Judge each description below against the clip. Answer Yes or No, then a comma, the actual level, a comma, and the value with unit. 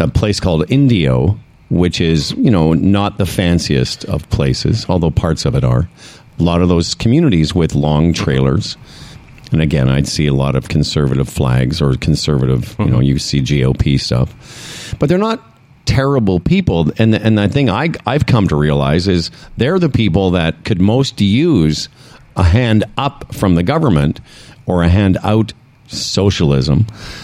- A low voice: Yes, very low, 90 Hz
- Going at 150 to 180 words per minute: Yes, average, 170 wpm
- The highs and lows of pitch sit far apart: Yes, wide, 6.8 semitones